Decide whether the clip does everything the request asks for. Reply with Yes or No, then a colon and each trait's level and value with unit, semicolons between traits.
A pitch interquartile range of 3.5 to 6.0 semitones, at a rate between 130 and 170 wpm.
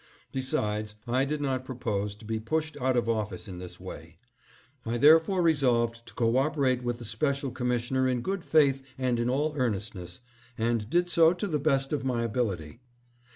No: average, 3.9 semitones; average, 185 wpm